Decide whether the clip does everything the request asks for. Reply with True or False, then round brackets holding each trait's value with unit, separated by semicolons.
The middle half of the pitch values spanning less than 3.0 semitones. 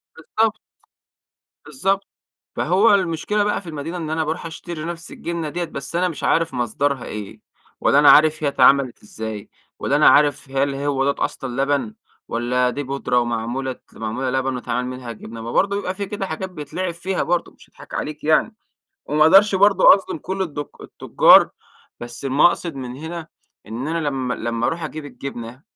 False (5.2 semitones)